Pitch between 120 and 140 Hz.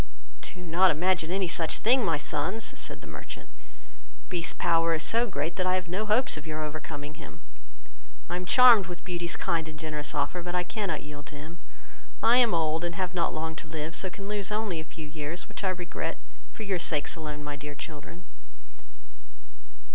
No: medium, 170 Hz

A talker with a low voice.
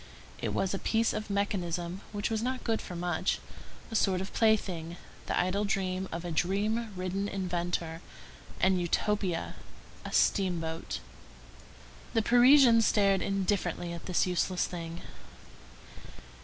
No: high, 190 Hz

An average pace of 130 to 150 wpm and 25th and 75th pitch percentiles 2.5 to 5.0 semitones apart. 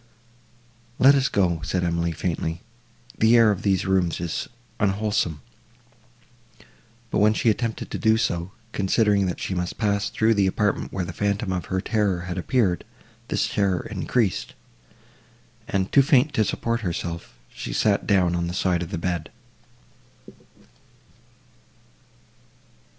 Yes: average, 140 wpm; average, 3.5 semitones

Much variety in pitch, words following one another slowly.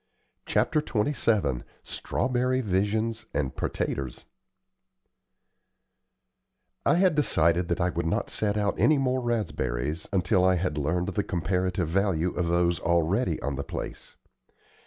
No: average, 5.0 semitones; slow, 125 wpm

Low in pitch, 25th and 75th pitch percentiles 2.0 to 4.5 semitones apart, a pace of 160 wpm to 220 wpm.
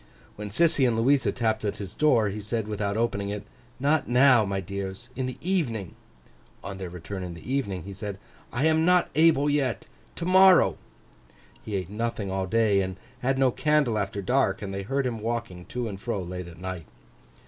No: low, 110 Hz; average, 5.3 semitones; average, 190 wpm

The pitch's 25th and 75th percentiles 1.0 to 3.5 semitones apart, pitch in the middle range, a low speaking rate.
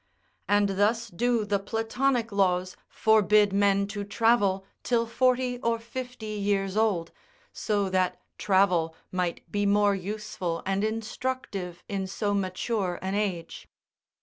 No: average, 2.8 semitones; high, 205 Hz; slow, 125 wpm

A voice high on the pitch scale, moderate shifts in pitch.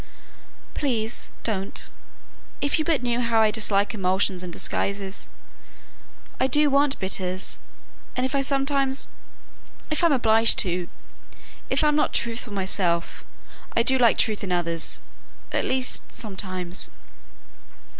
No: high, 225 Hz; wide, 5.8 semitones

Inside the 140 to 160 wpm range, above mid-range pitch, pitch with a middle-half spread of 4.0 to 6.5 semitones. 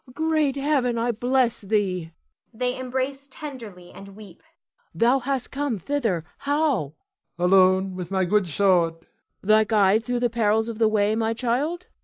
Yes: average, 155 wpm; high, 225 Hz; average, 5.1 semitones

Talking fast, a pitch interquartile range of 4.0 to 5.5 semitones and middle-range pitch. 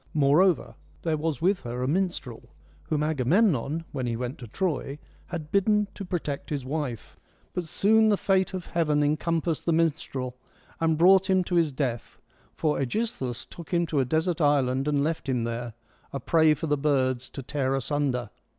No: average, 180 wpm; average, 4.6 semitones; medium, 150 Hz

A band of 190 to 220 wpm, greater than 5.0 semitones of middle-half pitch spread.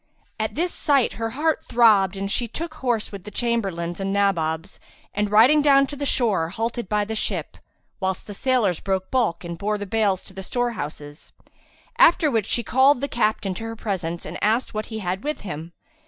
No: average, 200 wpm; average, 4.2 semitones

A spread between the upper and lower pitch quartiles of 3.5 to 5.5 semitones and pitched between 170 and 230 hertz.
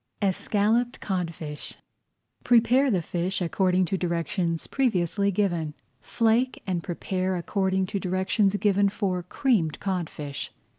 No: average, 3.1 semitones; high, 190 Hz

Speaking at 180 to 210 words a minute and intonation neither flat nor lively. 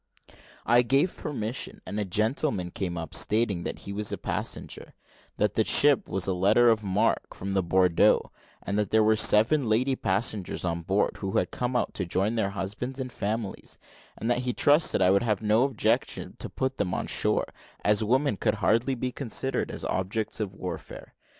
Yes: average, 185 wpm; average, 4.1 semitones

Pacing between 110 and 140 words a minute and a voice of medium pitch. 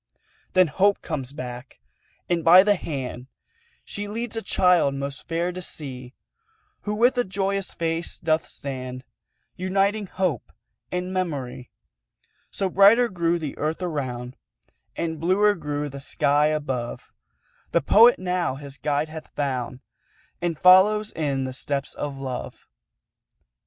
Yes: slow, 135 wpm; medium, 160 Hz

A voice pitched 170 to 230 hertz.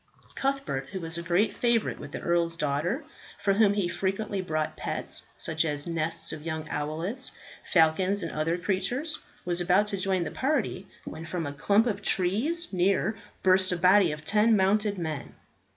Yes: medium, 185 Hz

